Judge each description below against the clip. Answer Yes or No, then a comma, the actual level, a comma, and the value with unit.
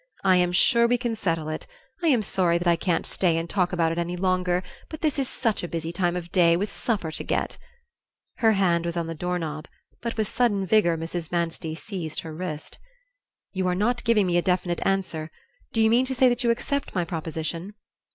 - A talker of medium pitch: Yes, medium, 180 Hz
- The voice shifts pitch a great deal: No, average, 4.4 semitones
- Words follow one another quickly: Yes, fast, 225 wpm